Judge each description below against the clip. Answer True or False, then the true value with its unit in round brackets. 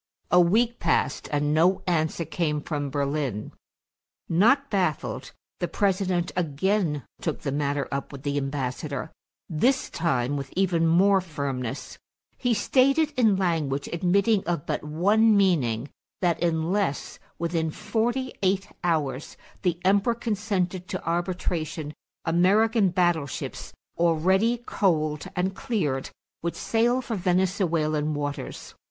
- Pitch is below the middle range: False (175 Hz)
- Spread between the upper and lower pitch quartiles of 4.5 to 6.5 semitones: True (4.9 semitones)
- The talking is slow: True (120 wpm)